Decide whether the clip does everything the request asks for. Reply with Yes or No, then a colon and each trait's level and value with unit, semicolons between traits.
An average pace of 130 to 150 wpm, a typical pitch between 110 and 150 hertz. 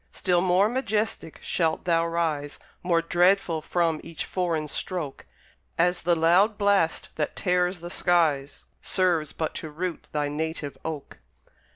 No: average, 140 wpm; medium, 170 Hz